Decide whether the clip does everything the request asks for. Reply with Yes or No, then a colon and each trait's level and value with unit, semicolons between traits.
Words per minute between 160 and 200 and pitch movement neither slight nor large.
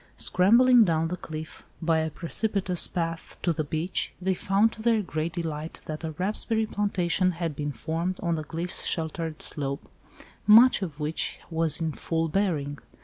Yes: average, 165 wpm; average, 3.3 semitones